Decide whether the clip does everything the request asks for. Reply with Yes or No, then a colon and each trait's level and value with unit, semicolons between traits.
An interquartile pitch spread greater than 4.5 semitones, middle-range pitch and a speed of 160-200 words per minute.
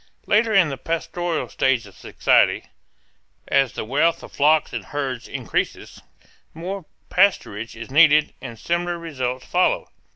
No: average, 4.9 semitones; medium, 150 Hz; slow, 135 wpm